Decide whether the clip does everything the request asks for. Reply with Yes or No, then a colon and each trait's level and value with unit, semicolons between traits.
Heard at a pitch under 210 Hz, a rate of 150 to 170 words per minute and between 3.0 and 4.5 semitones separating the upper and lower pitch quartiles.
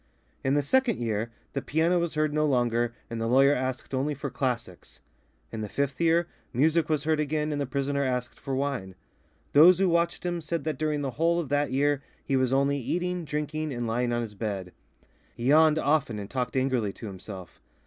No: medium, 140 Hz; fast, 205 wpm; average, 4.2 semitones